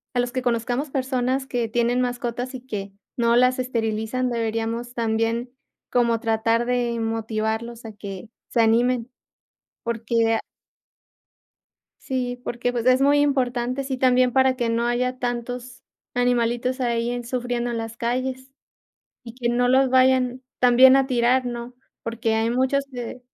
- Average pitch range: No, narrow, 1.6 semitones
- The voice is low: No, high, 245 Hz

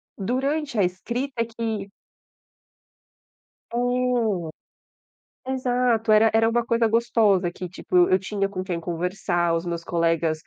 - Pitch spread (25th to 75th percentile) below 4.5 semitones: No, average, 4.9 semitones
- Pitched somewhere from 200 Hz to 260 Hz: Yes, high, 215 Hz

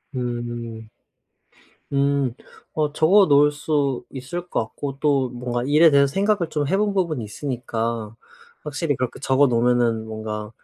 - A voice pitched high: No, low, 135 Hz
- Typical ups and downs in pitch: Yes, average, 4.0 semitones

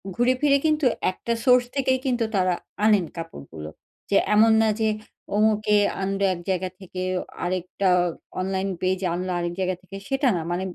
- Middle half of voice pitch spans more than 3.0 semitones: Yes, average, 4.3 semitones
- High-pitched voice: Yes, high, 195 Hz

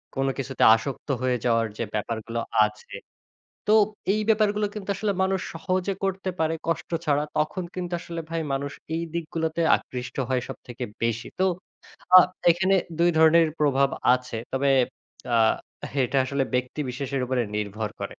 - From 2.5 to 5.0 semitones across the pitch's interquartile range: No, wide, 5.5 semitones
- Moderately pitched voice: Yes, medium, 145 Hz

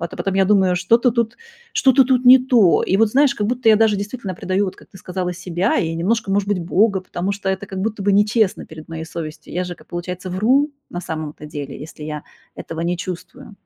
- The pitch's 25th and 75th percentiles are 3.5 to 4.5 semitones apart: Yes, average, 4.0 semitones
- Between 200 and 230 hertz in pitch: No, high, 190 Hz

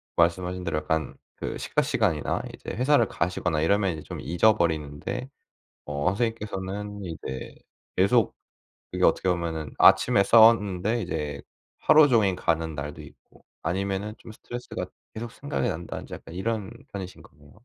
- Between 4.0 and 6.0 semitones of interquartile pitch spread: Yes, average, 5.1 semitones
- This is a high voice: No, very low, 95 Hz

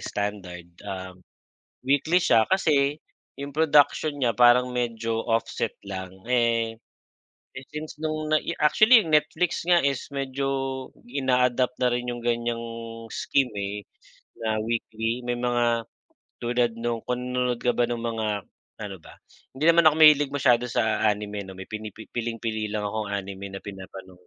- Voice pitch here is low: Yes, low, 120 Hz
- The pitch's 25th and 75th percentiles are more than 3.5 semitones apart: Yes, average, 4.1 semitones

